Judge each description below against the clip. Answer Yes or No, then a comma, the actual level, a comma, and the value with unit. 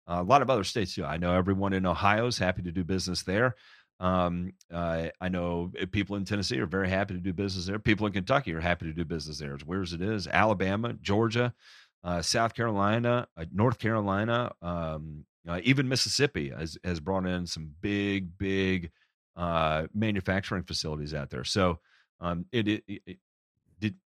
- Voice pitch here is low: Yes, very low, 95 Hz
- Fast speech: No, average, 180 wpm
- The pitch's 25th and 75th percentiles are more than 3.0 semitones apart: Yes, average, 3.5 semitones